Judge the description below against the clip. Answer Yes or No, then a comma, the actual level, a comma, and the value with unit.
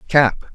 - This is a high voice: No, low, 135 Hz